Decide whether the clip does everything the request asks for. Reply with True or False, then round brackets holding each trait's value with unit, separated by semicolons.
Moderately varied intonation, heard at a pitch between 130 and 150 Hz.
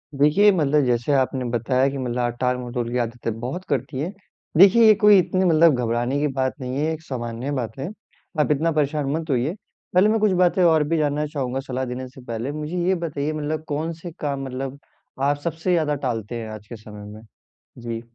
True (4.2 semitones; 140 Hz)